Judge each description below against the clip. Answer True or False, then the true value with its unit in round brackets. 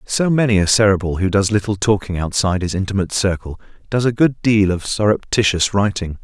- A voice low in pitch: True (100 Hz)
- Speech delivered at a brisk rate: False (185 wpm)